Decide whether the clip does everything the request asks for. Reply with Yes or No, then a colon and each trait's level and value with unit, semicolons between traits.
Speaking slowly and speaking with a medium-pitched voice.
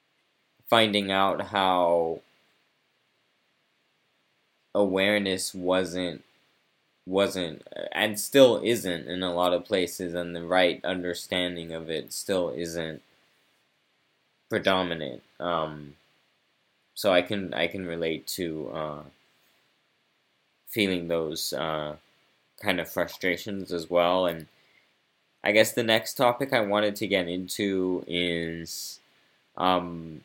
No: slow, 105 wpm; very low, 90 Hz